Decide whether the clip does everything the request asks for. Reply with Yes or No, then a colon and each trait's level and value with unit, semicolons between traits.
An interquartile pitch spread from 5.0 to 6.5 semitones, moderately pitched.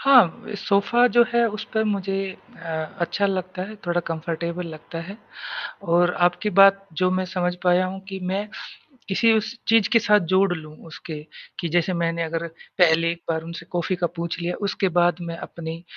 No: average, 2.9 semitones; medium, 180 Hz